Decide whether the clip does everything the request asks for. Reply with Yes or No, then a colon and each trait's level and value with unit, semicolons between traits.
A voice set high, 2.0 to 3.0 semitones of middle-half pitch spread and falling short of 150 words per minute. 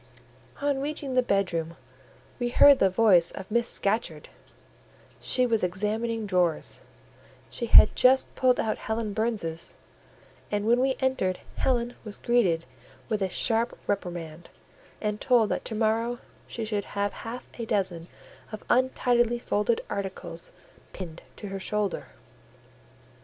No: high, 215 Hz; average, 3.9 semitones; slow, 135 wpm